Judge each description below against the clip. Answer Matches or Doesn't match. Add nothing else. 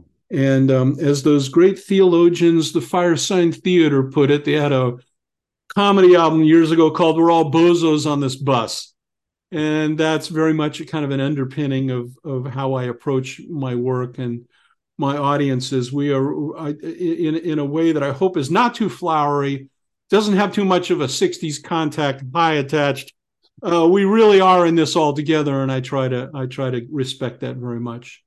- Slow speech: Doesn't match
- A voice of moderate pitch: Matches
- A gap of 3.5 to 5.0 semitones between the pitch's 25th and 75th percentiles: Matches